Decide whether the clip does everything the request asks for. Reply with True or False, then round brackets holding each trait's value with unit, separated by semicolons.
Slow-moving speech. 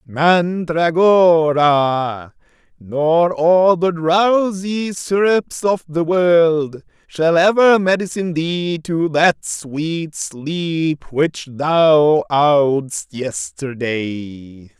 True (85 wpm)